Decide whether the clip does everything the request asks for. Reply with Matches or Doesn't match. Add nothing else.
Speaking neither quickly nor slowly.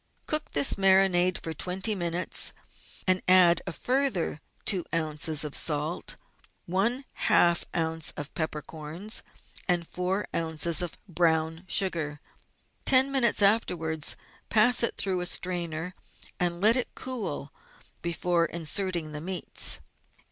Doesn't match